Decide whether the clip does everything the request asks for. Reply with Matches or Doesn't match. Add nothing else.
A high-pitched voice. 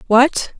Matches